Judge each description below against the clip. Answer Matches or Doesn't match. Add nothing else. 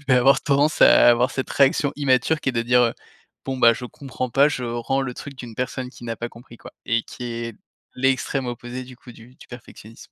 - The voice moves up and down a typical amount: Doesn't match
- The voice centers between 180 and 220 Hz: Doesn't match